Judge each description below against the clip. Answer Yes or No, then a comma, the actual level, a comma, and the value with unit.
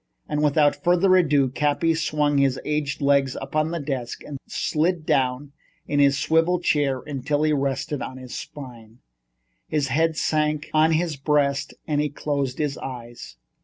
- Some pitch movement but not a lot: No, narrow, 2.1 semitones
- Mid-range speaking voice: Yes, medium, 145 Hz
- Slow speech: No, average, 165 wpm